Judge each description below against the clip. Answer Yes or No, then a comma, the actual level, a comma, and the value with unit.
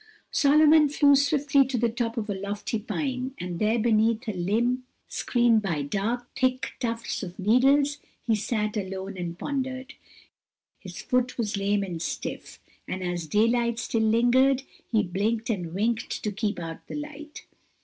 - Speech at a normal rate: Yes, average, 160 wpm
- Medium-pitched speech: No, high, 230 Hz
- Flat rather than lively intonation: No, average, 4.3 semitones